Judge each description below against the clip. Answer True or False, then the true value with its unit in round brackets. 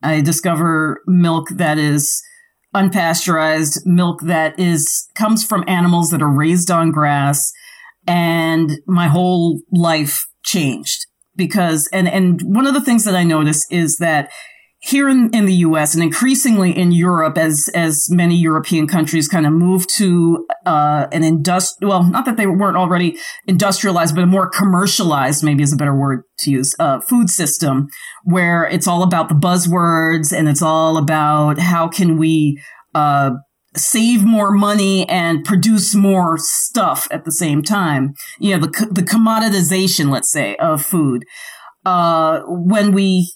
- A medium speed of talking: True (155 wpm)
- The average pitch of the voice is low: False (170 Hz)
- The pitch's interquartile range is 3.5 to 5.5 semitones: False (3.1 semitones)